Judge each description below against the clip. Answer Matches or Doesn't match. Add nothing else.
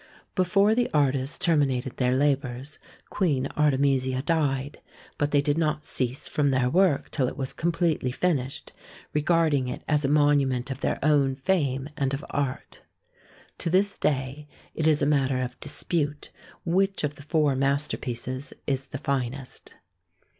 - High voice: Doesn't match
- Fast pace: Doesn't match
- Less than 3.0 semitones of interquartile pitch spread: Matches